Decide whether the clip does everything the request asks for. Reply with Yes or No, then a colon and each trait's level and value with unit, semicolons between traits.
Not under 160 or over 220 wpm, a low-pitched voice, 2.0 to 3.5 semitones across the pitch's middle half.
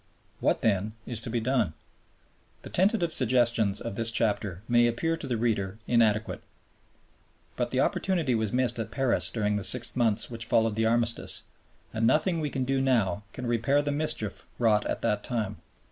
Yes: average, 175 wpm; low, 115 Hz; average, 3.0 semitones